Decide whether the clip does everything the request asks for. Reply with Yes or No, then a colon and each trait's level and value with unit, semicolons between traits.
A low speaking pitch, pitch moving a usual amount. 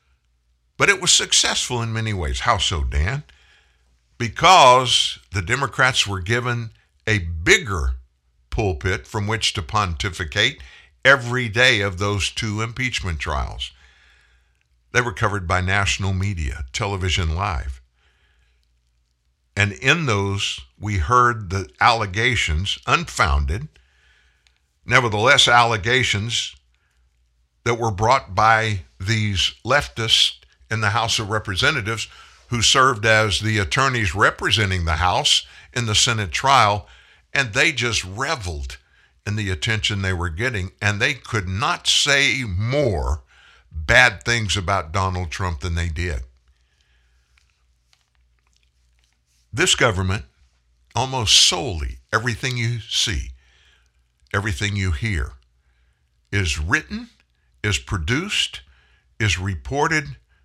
No: very low, 95 Hz; wide, 8.9 semitones